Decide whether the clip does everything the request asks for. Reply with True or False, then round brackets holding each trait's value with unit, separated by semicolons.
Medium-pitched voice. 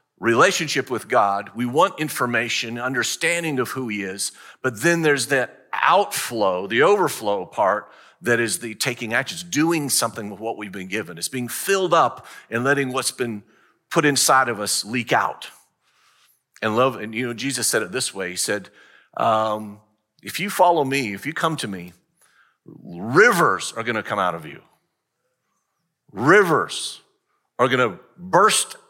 False (120 Hz)